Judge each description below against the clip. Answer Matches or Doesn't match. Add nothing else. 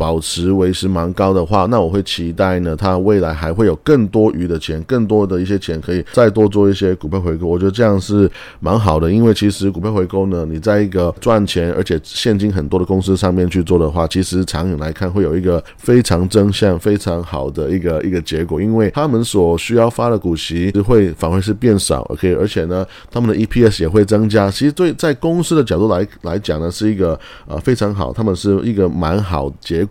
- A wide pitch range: Doesn't match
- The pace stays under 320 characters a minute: Doesn't match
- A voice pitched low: Matches